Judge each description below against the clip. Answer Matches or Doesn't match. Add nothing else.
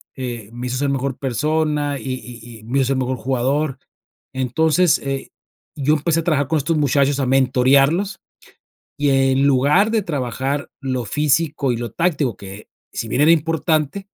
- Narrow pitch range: Doesn't match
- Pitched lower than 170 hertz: Matches